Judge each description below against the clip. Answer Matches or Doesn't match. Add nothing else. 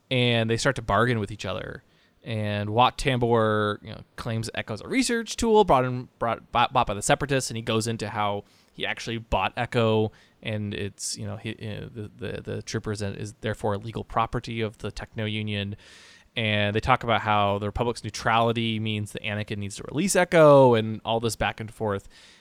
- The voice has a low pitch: Matches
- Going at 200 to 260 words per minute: Matches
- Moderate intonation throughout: Doesn't match